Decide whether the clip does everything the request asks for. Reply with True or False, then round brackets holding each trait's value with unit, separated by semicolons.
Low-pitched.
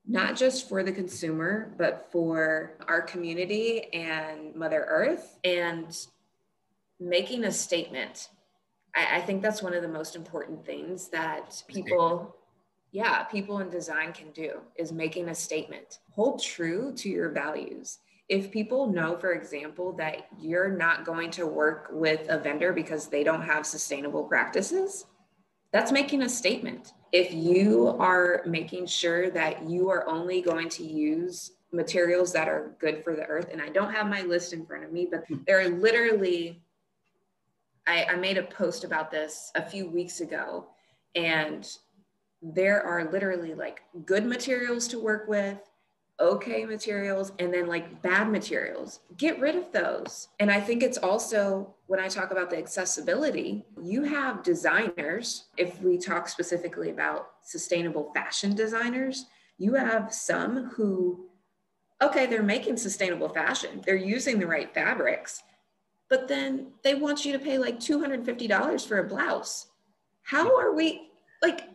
False (185 Hz)